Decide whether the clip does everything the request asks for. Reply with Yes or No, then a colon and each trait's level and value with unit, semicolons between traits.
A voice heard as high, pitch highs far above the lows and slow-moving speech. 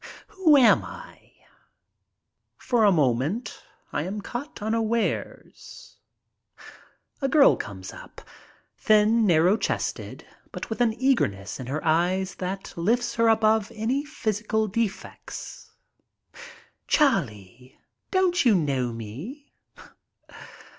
Yes: high, 215 Hz; wide, 7.3 semitones; slow, 110 wpm